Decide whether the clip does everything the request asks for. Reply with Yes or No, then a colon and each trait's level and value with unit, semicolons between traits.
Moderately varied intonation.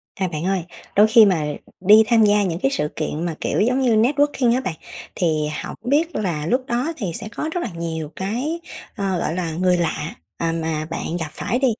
No: wide, 6.8 semitones